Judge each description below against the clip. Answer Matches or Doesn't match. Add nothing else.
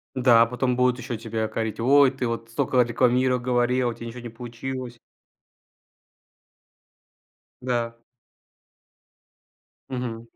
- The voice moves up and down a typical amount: Doesn't match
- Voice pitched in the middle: Doesn't match